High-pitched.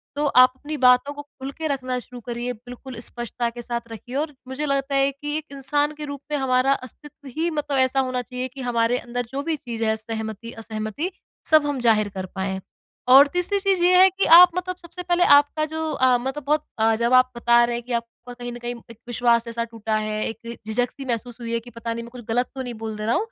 Yes: very high, 250 Hz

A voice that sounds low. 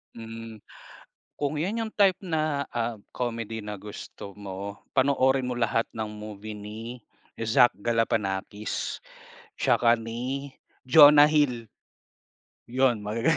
Yes: low, 115 Hz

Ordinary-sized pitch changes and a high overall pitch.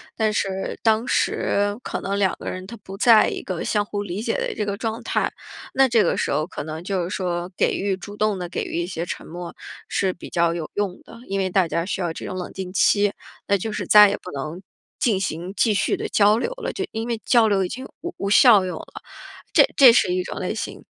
Yes: average, 3.2 semitones; high, 195 Hz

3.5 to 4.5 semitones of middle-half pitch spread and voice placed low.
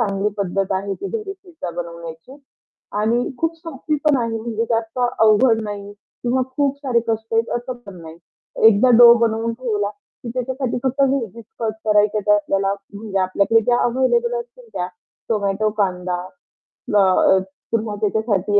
No: average, 3.8 semitones; high, 220 Hz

